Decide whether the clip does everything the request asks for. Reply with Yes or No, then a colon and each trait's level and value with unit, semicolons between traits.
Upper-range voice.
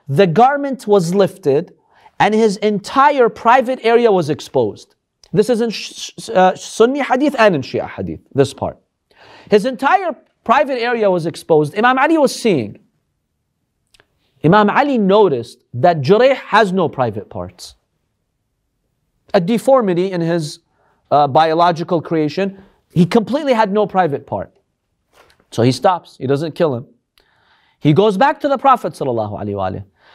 Yes: high, 195 Hz